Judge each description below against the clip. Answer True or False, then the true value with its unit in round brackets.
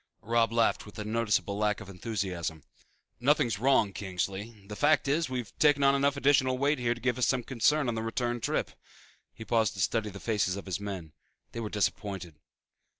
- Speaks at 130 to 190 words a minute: False (200 wpm)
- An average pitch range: True (4.1 semitones)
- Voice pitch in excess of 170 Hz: False (115 Hz)